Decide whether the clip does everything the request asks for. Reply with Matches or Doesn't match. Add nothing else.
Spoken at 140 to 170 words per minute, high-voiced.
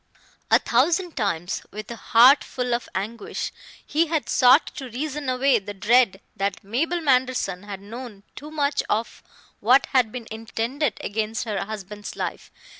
Matches